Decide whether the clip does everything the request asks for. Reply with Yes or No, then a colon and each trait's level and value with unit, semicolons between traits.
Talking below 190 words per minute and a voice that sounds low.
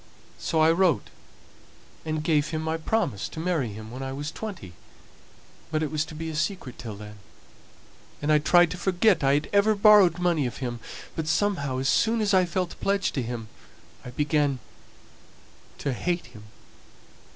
No: average, 175 wpm; medium, 155 Hz